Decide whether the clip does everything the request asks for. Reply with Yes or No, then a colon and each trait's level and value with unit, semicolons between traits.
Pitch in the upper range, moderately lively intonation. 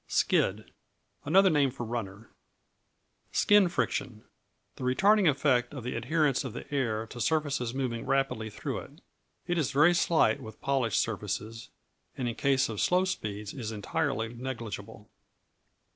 No: low, 125 Hz; average, 4.5 semitones